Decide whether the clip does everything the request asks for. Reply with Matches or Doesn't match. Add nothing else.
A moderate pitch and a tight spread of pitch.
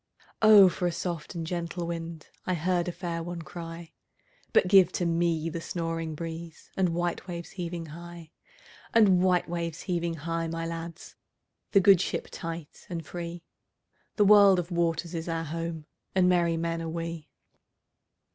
Matches